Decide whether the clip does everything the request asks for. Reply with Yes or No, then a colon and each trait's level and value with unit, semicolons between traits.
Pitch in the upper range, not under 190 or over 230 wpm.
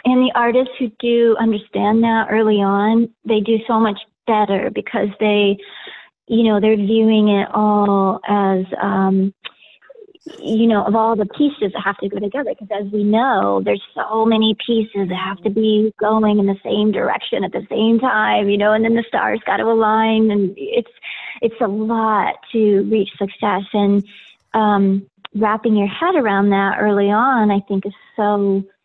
No: high, 215 Hz; average, 180 wpm